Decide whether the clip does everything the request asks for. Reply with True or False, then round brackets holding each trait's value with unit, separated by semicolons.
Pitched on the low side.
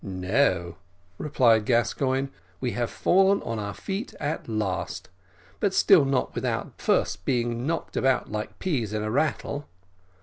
True (125 Hz)